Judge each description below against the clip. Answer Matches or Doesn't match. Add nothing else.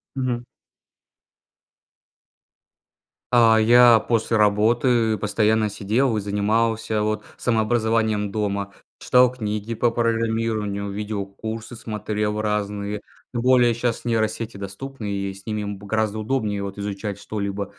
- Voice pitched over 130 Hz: Doesn't match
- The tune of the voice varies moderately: Doesn't match